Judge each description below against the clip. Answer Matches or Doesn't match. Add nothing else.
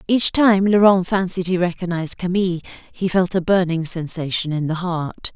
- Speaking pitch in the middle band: Matches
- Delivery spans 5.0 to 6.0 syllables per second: Matches